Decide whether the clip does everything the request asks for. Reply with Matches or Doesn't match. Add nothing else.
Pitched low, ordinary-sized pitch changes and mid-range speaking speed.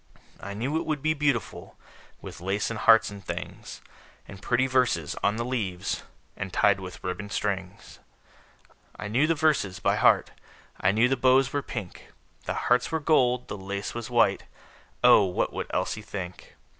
Matches